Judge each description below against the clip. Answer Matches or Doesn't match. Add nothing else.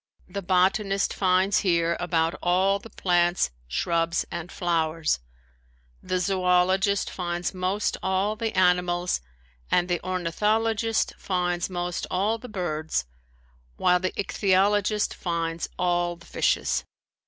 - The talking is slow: Matches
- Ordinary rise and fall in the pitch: Doesn't match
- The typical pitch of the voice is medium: Matches